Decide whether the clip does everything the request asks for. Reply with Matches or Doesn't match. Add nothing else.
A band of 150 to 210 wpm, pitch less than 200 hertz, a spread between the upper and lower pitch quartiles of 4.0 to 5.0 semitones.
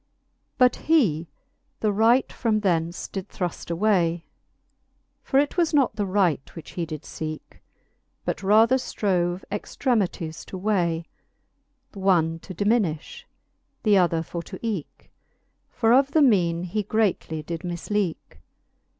Doesn't match